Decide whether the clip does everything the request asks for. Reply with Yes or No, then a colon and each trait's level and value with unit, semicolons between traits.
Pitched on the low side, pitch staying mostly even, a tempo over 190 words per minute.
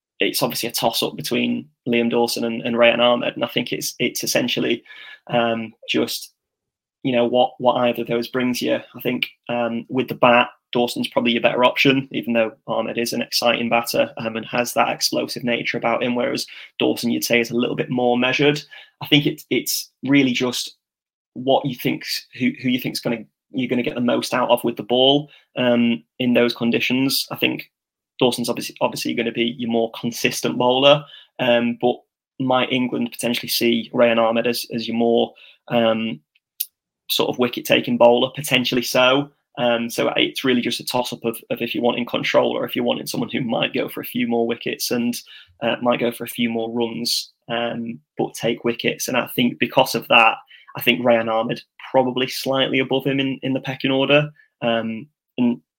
Yes: low, 120 Hz; narrow, 1.6 semitones; average, 200 wpm